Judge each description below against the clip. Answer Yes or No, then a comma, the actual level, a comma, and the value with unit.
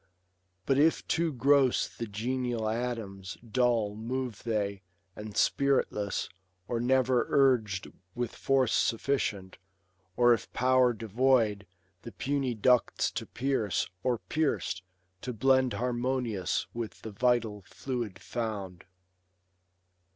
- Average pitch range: Yes, average, 3.4 semitones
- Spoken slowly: Yes, slow, 110 wpm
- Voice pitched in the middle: No, low, 120 Hz